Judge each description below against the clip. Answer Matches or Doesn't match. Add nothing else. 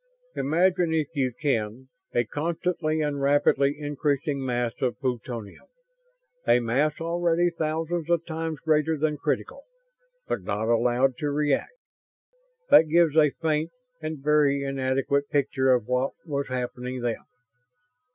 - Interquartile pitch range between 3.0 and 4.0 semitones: Matches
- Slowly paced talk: Matches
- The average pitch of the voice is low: Doesn't match